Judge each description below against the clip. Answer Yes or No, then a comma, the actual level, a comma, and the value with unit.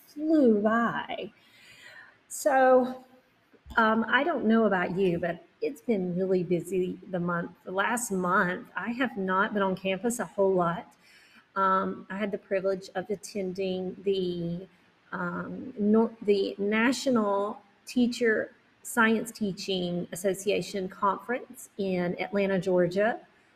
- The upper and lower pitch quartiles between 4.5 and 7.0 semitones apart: No, average, 3.4 semitones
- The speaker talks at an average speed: No, slow, 120 wpm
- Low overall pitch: No, high, 200 Hz